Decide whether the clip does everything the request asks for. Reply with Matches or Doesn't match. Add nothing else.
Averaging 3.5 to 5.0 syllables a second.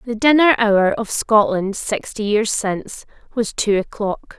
Matches